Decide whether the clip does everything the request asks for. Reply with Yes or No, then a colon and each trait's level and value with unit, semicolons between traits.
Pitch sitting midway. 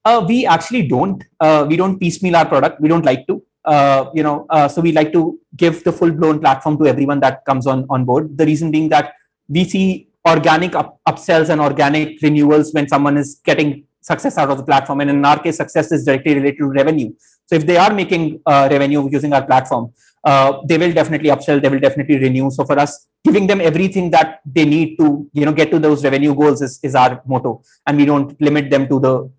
Yes: medium, 150 Hz